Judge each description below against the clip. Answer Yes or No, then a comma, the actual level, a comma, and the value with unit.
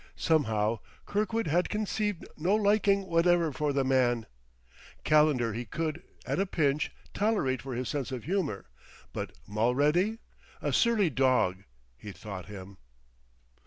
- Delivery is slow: Yes, slow, 130 wpm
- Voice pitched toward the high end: No, medium, 145 Hz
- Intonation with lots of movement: Yes, wide, 7.8 semitones